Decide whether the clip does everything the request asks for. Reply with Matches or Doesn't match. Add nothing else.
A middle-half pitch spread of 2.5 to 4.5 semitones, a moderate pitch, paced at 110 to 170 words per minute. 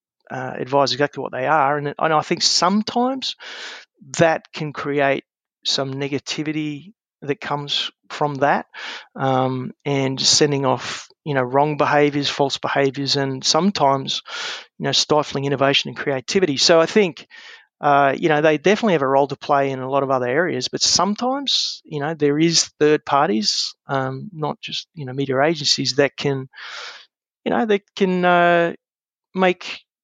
Matches